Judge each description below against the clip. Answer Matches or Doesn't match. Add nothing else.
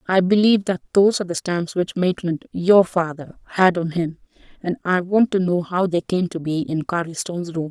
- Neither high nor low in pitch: Matches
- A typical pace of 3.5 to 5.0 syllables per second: Doesn't match